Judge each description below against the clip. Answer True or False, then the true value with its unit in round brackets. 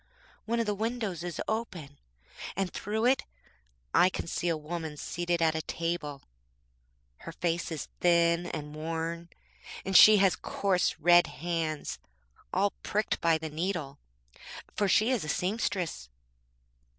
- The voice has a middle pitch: True (175 Hz)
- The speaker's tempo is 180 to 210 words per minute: False (140 wpm)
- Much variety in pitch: False (3.5 semitones)